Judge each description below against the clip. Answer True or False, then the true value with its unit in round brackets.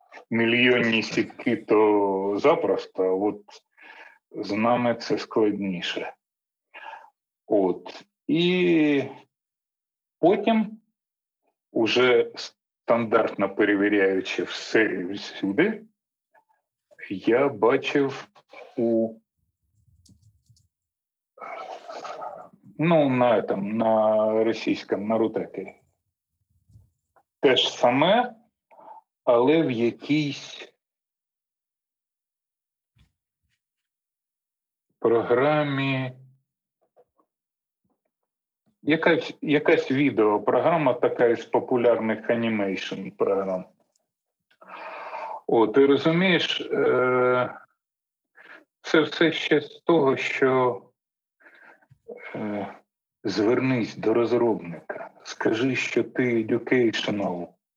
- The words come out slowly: True (60 wpm)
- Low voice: True (120 Hz)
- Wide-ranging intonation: True (6.3 semitones)